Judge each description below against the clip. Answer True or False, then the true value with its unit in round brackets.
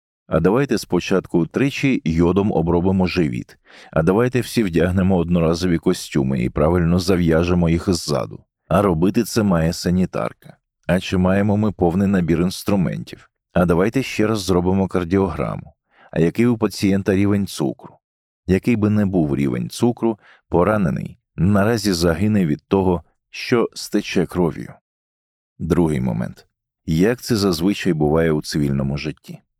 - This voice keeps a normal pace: False (130 wpm)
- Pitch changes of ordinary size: True (3.3 semitones)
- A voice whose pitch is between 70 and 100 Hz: True (95 Hz)